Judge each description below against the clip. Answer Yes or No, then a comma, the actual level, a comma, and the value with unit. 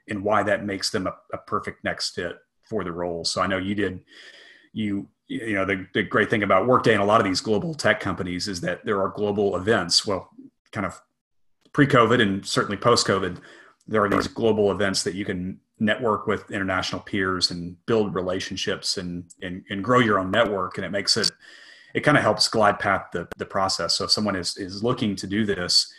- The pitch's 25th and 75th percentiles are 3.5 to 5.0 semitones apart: No, narrow, 2.4 semitones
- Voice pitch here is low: Yes, low, 100 Hz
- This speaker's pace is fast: Yes, fast, 215 wpm